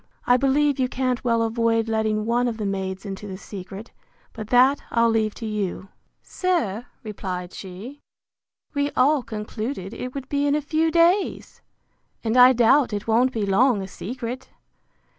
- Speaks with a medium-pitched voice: No, high, 230 Hz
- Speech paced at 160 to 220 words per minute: Yes, average, 165 wpm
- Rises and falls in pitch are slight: No, average, 3.8 semitones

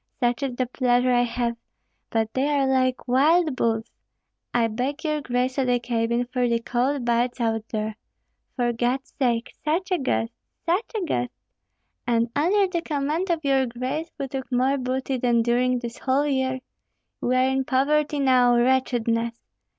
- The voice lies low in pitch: No, very high, 255 Hz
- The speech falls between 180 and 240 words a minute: No, average, 170 wpm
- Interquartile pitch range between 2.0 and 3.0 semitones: Yes, narrow, 2.5 semitones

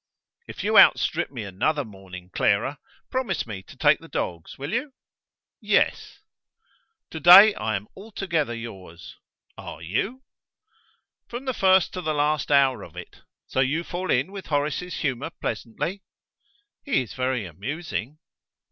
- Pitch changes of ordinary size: No, wide, 8.5 semitones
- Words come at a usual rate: Yes, average, 145 wpm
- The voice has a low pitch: No, medium, 145 Hz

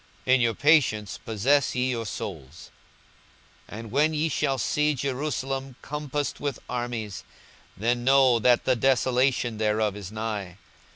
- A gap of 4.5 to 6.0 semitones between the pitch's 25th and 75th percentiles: No, average, 3.9 semitones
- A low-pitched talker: Yes, low, 125 Hz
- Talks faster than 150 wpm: No, average, 140 wpm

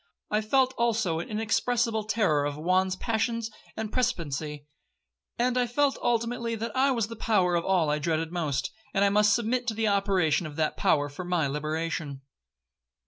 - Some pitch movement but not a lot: No, wide, 6.2 semitones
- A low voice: No, high, 200 Hz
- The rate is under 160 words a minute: No, average, 175 wpm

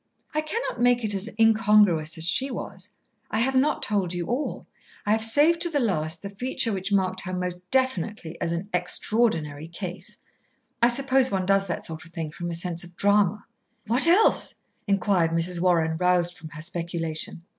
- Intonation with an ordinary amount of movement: Yes, average, 5.0 semitones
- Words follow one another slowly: No, average, 185 wpm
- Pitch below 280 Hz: Yes, high, 190 Hz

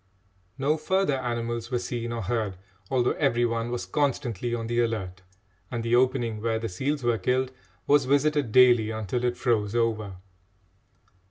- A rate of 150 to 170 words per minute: Yes, average, 160 wpm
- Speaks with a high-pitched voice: No, low, 120 Hz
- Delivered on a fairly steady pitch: Yes, narrow, 2.3 semitones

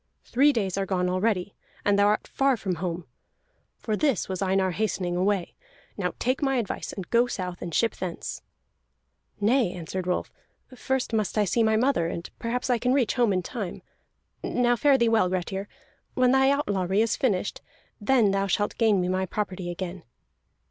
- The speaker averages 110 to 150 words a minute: No, average, 180 wpm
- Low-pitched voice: No, high, 205 Hz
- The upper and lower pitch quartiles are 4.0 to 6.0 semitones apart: Yes, average, 4.6 semitones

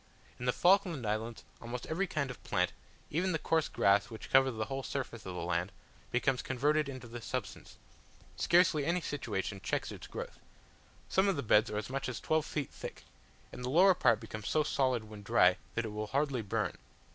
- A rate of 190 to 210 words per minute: Yes, average, 200 wpm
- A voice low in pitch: Yes, low, 125 Hz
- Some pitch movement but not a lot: No, wide, 5.7 semitones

